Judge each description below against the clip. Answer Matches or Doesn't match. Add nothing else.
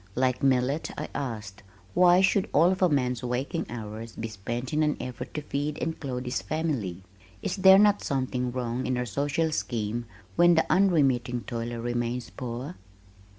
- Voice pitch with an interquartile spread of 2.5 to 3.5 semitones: Doesn't match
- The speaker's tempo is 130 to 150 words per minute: Doesn't match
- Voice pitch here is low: Matches